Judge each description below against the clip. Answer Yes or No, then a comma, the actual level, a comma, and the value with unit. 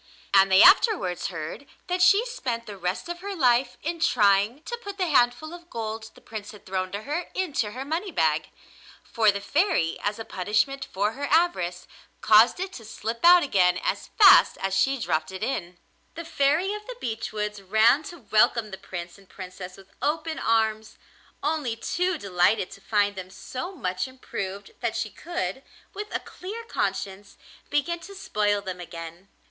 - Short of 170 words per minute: No, average, 180 wpm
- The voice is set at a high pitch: Yes, high, 225 Hz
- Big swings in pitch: Yes, wide, 8.8 semitones